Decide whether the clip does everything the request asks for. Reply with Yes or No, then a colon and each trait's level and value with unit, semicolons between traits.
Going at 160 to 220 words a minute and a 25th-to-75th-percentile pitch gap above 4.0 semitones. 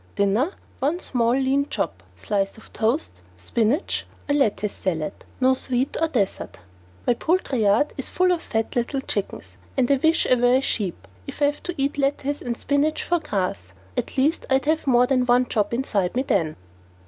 Yes: average, 185 wpm; average, 5.2 semitones